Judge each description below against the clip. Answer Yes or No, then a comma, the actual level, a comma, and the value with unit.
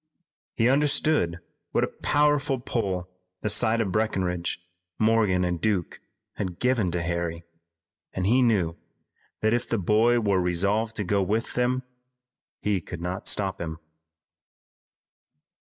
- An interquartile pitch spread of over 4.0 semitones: Yes, average, 4.5 semitones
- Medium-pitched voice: No, low, 105 Hz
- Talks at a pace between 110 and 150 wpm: Yes, slow, 135 wpm